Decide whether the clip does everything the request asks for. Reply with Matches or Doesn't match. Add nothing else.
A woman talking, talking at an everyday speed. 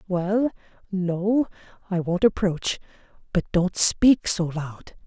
Doesn't match